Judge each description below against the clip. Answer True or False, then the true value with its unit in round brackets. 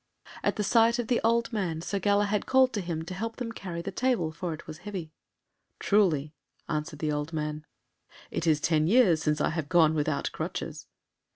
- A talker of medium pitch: True (175 Hz)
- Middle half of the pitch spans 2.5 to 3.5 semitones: False (5.3 semitones)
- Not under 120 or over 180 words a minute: False (195 wpm)